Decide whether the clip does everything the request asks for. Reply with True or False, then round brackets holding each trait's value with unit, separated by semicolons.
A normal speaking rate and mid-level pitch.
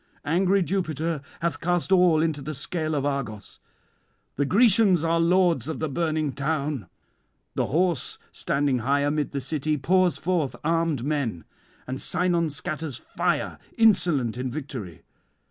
True (145 wpm; 155 Hz)